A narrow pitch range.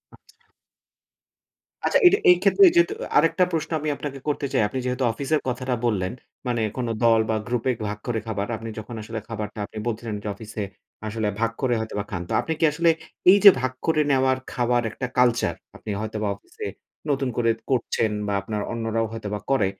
No: average, 3.4 semitones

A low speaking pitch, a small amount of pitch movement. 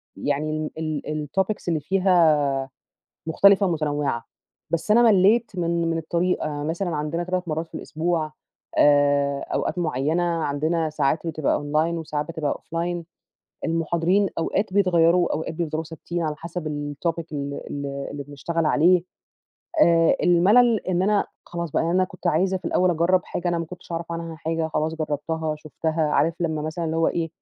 No: medium, 165 Hz; narrow, 2.3 semitones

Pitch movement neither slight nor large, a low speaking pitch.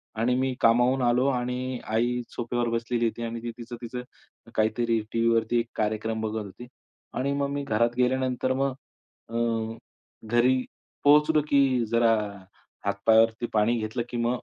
No: narrow, 1.9 semitones; low, 120 Hz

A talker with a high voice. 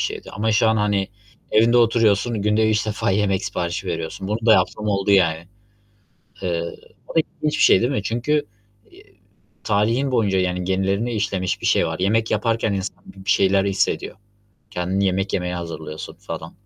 No: low, 100 Hz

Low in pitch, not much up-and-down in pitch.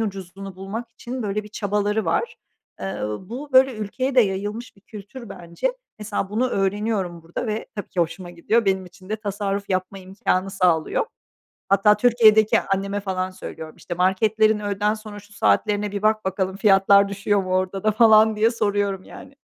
No: high, 205 Hz; narrow, 2.2 semitones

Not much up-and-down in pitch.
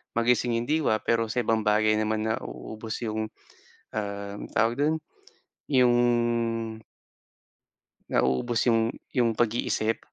Yes: narrow, 1.8 semitones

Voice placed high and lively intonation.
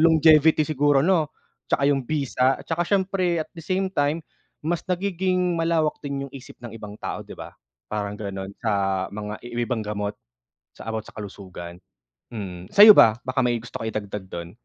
No: low, 135 Hz; wide, 7.8 semitones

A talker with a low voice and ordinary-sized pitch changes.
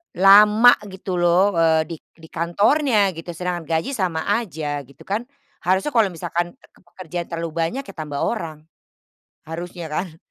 No: medium, 175 Hz; average, 3.5 semitones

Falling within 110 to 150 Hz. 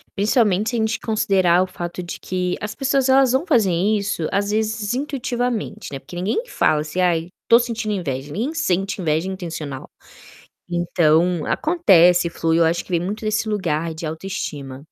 No: high, 190 Hz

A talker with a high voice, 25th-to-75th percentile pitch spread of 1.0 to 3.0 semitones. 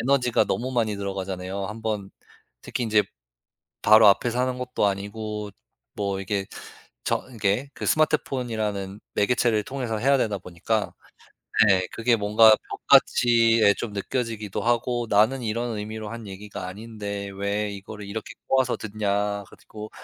No: low, 110 Hz; narrow, 2.6 semitones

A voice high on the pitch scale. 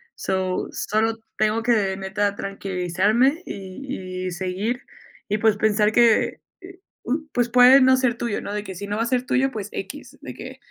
Yes: high, 215 Hz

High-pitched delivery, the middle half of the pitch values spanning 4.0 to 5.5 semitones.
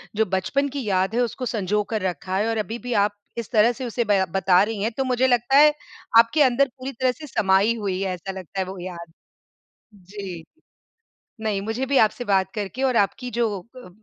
Yes: high, 215 Hz; average, 4.4 semitones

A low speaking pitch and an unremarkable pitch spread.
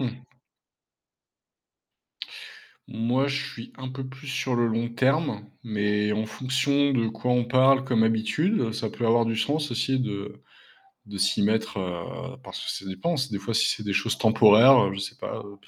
Yes: low, 115 Hz; average, 3.7 semitones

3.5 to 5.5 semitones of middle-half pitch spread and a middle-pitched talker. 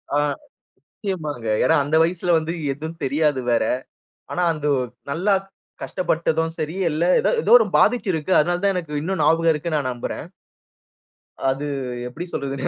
No: average, 3.1 semitones; medium, 160 Hz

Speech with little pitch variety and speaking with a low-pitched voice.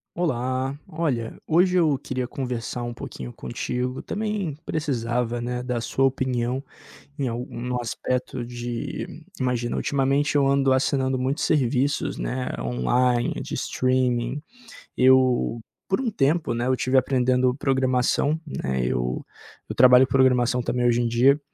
Yes: narrow, 2.1 semitones; low, 130 Hz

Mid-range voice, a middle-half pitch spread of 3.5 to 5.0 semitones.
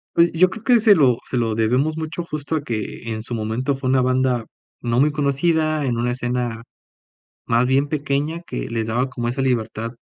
No: low, 130 Hz; average, 4.4 semitones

